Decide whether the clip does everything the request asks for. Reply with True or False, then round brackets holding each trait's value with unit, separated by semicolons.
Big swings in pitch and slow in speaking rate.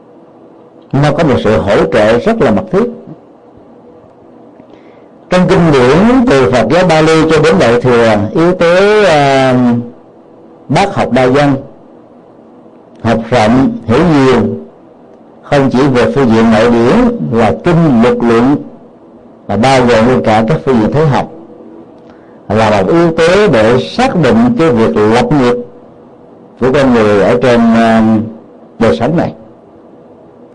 True (6.4 semitones; 140 wpm)